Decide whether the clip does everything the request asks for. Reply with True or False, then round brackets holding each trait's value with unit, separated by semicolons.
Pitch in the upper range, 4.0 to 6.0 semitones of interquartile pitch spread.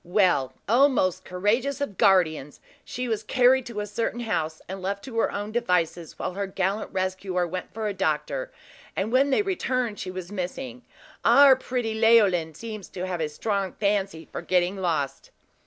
True (200 Hz; 4.5 semitones)